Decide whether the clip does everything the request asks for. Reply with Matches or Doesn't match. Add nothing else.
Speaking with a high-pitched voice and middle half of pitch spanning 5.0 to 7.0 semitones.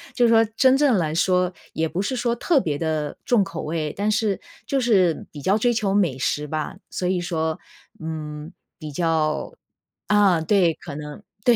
Doesn't match